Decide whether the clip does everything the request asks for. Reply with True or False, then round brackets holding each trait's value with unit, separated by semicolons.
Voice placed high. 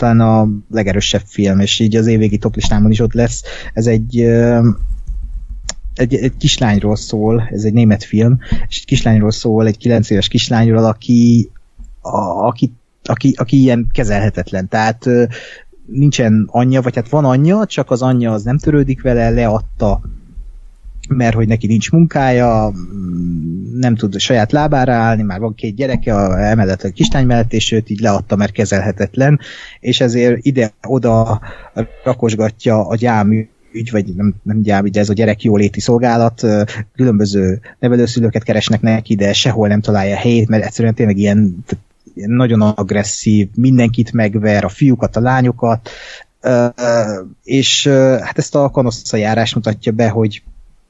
False (115 Hz)